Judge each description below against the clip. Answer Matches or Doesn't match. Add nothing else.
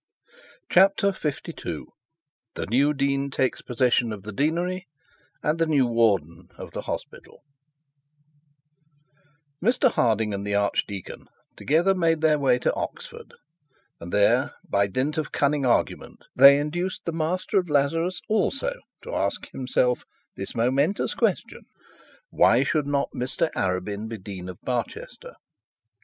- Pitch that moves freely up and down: Matches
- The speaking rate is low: Matches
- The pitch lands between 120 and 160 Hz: Matches